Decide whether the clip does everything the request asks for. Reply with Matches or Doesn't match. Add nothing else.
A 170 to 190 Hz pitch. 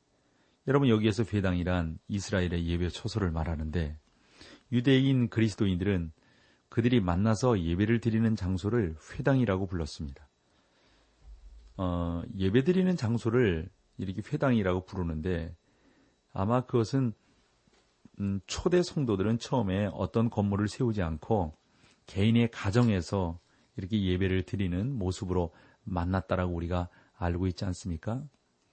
Doesn't match